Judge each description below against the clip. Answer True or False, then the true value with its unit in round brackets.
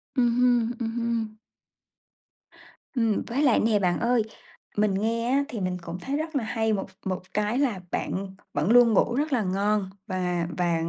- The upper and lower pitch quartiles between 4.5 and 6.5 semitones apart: False (4.0 semitones)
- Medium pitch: False (220 Hz)